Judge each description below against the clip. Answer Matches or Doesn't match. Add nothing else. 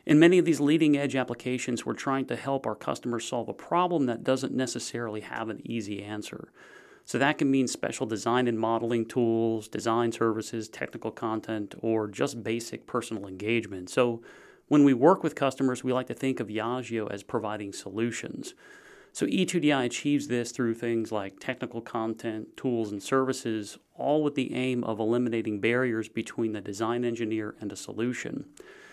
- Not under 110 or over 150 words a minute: Doesn't match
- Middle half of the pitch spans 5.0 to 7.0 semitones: Doesn't match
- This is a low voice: Matches